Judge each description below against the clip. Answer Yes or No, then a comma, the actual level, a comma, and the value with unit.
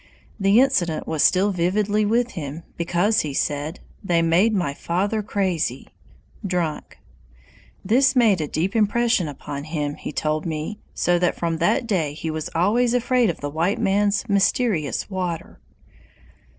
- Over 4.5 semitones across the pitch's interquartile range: Yes, average, 4.9 semitones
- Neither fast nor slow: Yes, average, 150 wpm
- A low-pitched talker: No, medium, 180 Hz